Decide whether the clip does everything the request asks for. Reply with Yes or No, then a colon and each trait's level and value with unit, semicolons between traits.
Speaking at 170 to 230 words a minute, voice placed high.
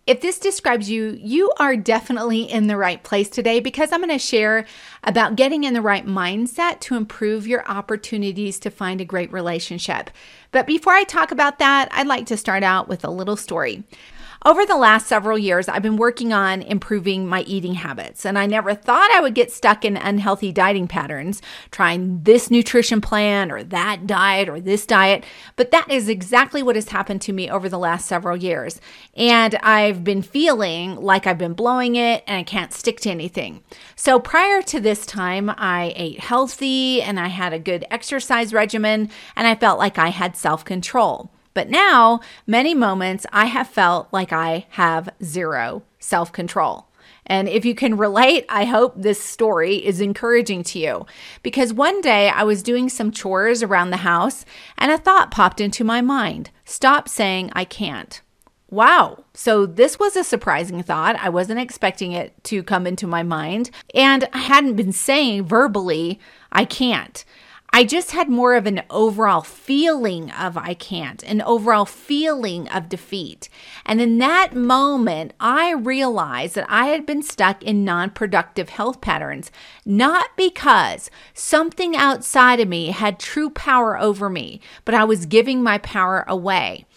Yes: average, 175 wpm; high, 215 Hz